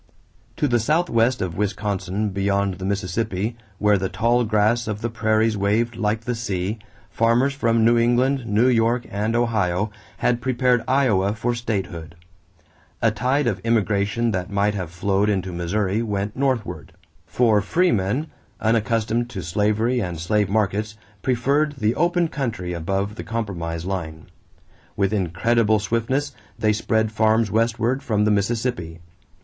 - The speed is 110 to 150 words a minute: Yes, average, 145 wpm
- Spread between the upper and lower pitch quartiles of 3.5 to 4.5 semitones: No, average, 3.1 semitones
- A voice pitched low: Yes, low, 110 Hz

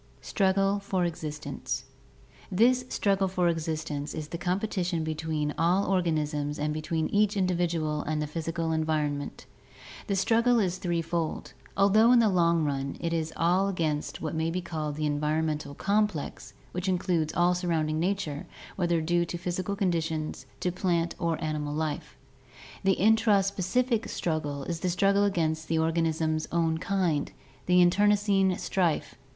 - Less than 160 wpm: Yes, average, 145 wpm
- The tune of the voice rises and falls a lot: No, average, 3.4 semitones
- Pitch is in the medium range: Yes, medium, 170 Hz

